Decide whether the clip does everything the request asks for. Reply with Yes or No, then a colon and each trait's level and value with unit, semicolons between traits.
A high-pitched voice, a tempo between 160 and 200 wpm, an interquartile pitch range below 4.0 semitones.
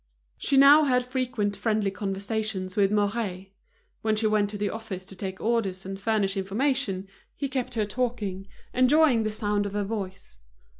Yes: high, 210 Hz; average, 165 wpm; average, 3.3 semitones